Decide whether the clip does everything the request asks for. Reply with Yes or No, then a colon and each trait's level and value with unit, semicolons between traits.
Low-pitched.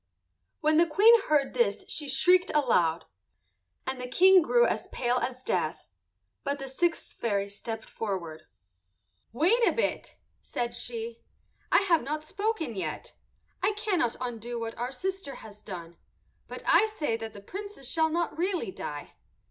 No: very high, 265 Hz